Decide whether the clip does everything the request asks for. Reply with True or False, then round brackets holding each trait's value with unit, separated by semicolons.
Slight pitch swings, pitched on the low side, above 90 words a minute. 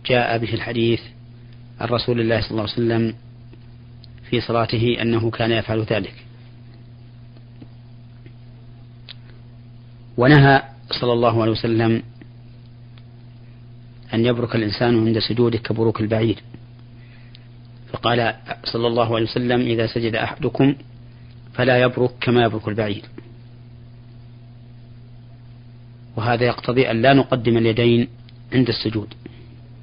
True (0.6 semitones; 120 Hz; 100 wpm)